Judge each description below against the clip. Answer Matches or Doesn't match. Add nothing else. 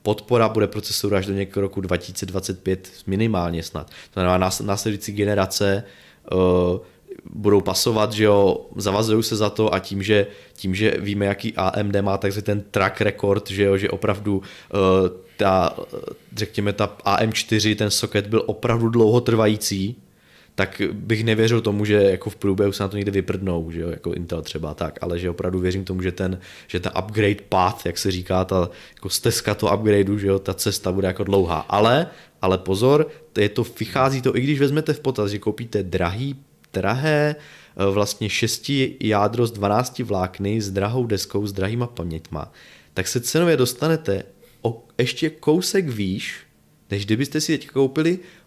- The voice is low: Matches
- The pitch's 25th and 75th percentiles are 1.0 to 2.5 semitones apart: Doesn't match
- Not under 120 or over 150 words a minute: Doesn't match